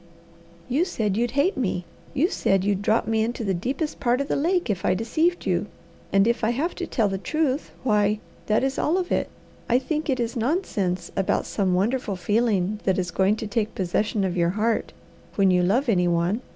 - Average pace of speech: No, fast, 210 wpm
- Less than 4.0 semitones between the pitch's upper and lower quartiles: No, average, 5.3 semitones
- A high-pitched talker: Yes, high, 220 Hz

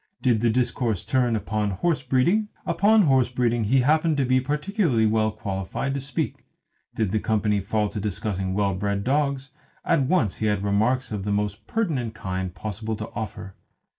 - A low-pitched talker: Yes, low, 115 Hz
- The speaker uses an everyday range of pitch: Yes, average, 4.5 semitones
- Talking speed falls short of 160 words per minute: No, average, 175 wpm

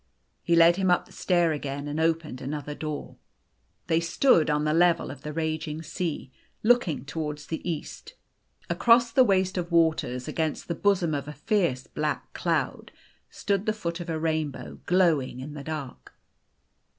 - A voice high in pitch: No, medium, 160 Hz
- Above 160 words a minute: Yes, average, 170 wpm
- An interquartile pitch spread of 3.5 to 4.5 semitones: No, average, 2.9 semitones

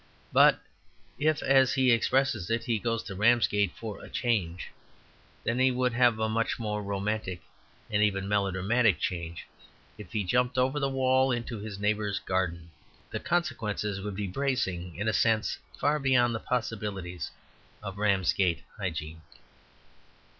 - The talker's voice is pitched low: Yes, low, 105 Hz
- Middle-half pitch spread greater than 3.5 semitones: Yes, average, 4.2 semitones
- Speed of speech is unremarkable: Yes, average, 145 wpm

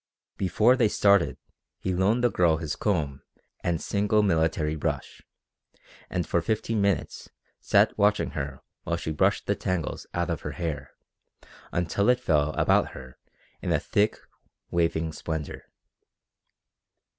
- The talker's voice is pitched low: Yes, very low, 85 Hz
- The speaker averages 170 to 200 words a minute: No, slow, 135 wpm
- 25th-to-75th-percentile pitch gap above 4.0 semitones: Yes, average, 4.4 semitones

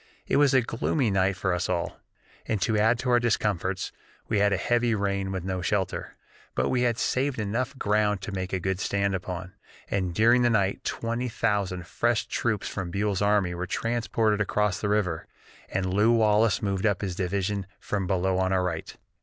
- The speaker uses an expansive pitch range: No, average, 3.2 semitones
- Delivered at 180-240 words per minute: Yes, average, 190 wpm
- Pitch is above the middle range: No, low, 100 Hz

